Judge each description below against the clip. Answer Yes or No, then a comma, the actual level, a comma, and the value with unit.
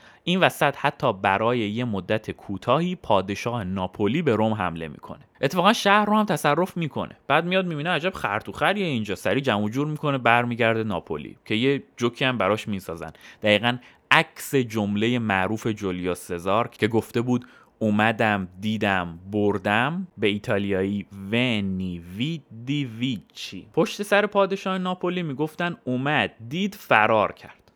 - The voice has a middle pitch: No, low, 115 Hz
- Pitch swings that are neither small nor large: No, wide, 6.7 semitones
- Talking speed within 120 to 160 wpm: Yes, average, 135 wpm